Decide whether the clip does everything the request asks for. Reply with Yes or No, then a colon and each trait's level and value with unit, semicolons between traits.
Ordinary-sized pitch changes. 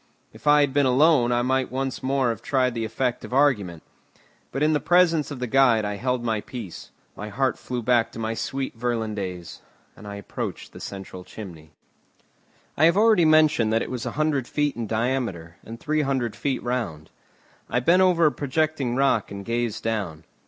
Yes: average, 4.4 semitones